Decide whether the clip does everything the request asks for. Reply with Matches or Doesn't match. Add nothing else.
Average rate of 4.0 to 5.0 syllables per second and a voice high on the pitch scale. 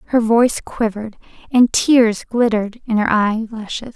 Matches